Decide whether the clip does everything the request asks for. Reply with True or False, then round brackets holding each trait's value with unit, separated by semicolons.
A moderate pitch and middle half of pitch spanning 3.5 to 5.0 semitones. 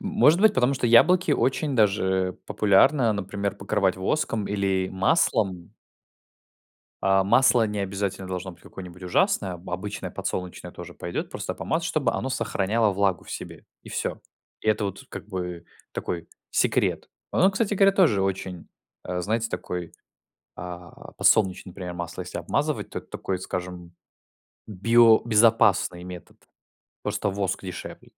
False (100 Hz; 3.9 semitones)